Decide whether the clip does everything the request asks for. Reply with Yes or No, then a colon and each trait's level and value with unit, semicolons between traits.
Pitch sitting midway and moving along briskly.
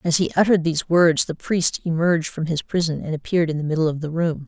Yes: medium, 165 Hz; fast, 255 wpm